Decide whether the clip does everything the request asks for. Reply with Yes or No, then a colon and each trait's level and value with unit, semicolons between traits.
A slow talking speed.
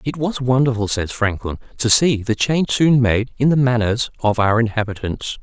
No: average, 190 wpm